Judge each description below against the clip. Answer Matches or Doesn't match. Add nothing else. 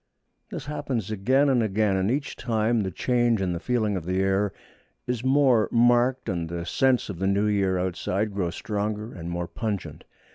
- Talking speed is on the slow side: Doesn't match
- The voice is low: Matches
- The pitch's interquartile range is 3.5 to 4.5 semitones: Matches